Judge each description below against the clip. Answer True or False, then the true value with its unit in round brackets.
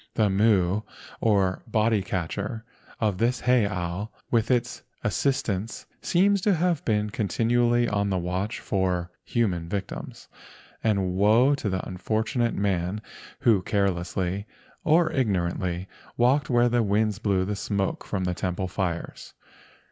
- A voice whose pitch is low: True (105 Hz)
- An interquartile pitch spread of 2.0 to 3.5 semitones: False (4.1 semitones)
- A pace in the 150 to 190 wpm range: False (135 wpm)